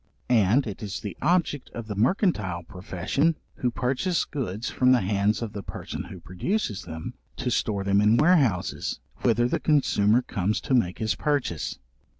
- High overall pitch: No, low, 110 Hz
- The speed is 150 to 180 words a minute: Yes, average, 165 wpm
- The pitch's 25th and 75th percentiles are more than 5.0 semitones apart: Yes, wide, 5.4 semitones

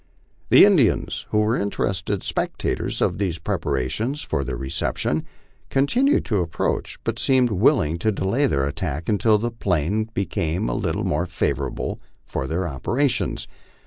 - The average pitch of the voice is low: Yes, very low, 95 Hz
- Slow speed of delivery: No, average, 145 wpm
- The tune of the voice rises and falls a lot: Yes, wide, 6.3 semitones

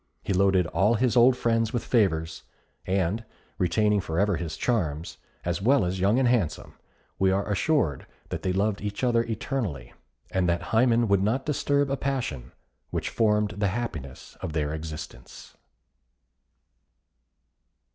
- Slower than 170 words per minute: Yes, average, 145 wpm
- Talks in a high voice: No, low, 100 Hz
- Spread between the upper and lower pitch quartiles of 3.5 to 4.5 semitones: No, average, 5.2 semitones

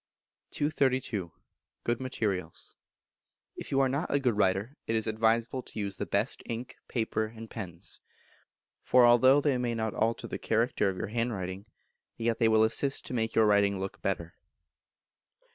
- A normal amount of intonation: Yes, average, 3.4 semitones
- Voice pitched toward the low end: Yes, low, 115 Hz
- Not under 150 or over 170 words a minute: Yes, average, 160 wpm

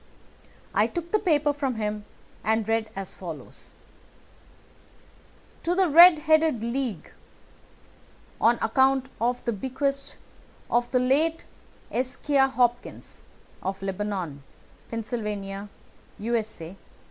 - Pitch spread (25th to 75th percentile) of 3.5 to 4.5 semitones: No, average, 4.9 semitones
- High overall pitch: Yes, high, 240 Hz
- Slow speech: Yes, slow, 100 wpm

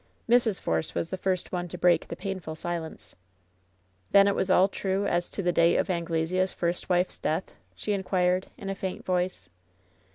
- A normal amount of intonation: No, narrow, 1.9 semitones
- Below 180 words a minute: No, average, 190 wpm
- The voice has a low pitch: No, medium, 180 Hz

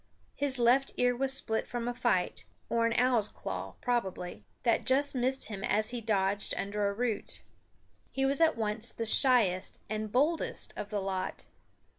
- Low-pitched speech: No, high, 230 Hz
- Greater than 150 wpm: Yes, average, 170 wpm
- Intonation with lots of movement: No, average, 3.6 semitones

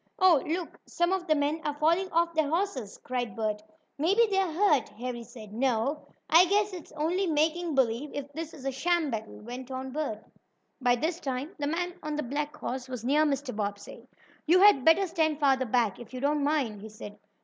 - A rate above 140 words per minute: Yes, fast, 205 wpm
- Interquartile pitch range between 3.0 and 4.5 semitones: No, average, 4.9 semitones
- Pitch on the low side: No, very high, 290 Hz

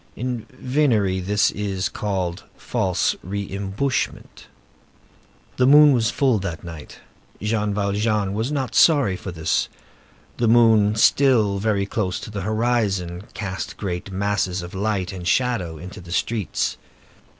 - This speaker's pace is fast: No, slow, 135 wpm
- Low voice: Yes, low, 105 Hz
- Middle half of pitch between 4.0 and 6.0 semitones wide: No, average, 3.5 semitones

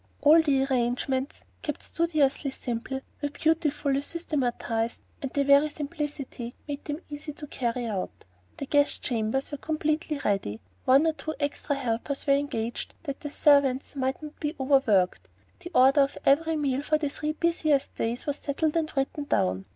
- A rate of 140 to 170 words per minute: Yes, average, 165 wpm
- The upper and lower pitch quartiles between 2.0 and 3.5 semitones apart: Yes, average, 2.7 semitones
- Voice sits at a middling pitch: No, very high, 280 Hz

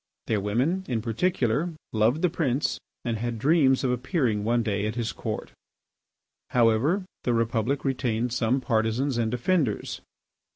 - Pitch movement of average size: Yes, average, 3.7 semitones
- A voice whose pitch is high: No, low, 120 Hz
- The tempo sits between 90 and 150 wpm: Yes, average, 140 wpm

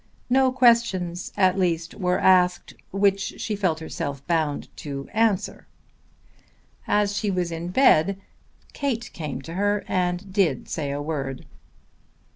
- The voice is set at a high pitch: No, medium, 180 Hz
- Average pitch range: Yes, average, 4.0 semitones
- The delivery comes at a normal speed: No, slow, 130 wpm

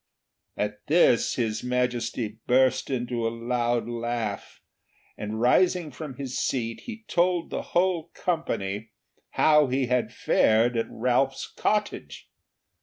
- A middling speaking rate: No, slow, 120 wpm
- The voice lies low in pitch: Yes, low, 125 Hz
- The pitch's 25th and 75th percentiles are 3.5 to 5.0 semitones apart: Yes, average, 4.7 semitones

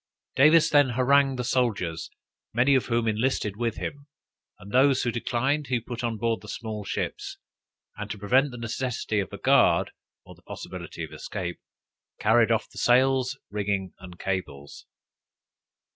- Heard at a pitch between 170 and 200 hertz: No, low, 120 Hz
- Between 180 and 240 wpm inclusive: No, average, 160 wpm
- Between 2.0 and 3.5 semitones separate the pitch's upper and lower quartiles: No, average, 4.0 semitones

